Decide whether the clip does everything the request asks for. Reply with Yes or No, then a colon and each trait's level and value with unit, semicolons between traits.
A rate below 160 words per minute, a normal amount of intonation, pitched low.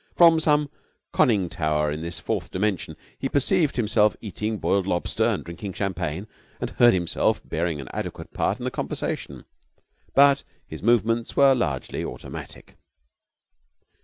No: average, 140 wpm; wide, 6.8 semitones; low, 105 Hz